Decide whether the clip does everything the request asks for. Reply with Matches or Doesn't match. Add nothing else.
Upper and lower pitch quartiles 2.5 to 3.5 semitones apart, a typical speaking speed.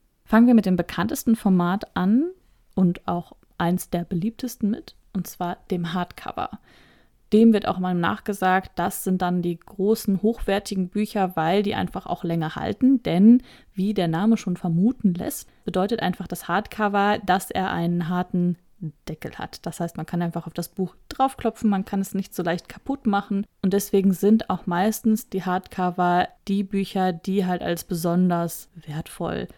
Matches